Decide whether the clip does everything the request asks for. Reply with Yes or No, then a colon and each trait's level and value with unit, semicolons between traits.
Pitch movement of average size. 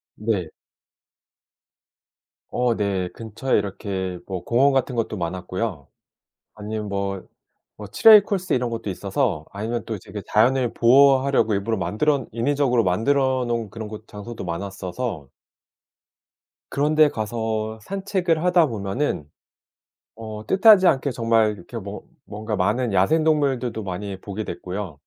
Yes: average, 4.9 semitones